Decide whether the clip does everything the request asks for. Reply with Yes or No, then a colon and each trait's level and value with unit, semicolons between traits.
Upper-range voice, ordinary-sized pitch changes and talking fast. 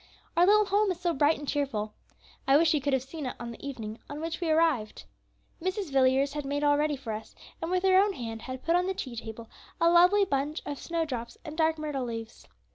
Yes: very high, 290 Hz; average, 4.6 semitones; fast, 235 wpm